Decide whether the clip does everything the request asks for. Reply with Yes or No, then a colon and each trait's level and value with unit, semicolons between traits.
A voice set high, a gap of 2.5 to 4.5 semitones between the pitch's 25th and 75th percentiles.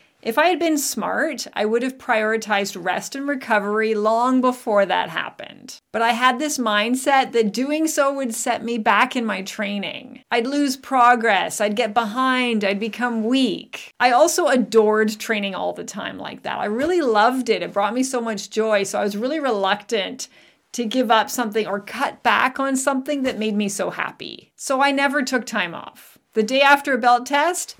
Yes: high, 240 Hz; average, 3.8 semitones